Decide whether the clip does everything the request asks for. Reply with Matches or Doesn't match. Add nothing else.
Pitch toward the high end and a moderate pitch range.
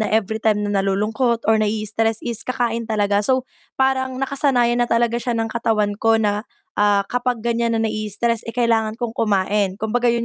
Doesn't match